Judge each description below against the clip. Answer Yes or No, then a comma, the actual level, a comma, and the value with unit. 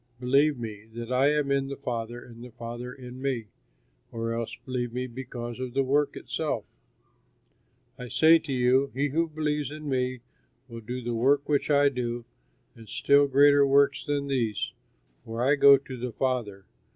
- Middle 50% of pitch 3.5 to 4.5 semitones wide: No, average, 2.9 semitones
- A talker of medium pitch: No, low, 130 Hz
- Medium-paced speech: Yes, average, 175 wpm